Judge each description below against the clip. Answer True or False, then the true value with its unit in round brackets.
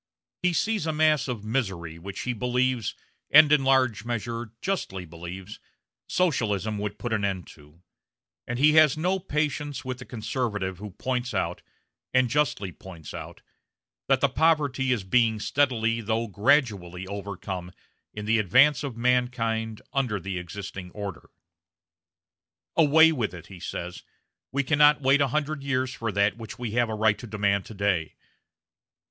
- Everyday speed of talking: True (155 wpm)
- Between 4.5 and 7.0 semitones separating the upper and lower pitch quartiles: True (5.2 semitones)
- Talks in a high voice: False (115 Hz)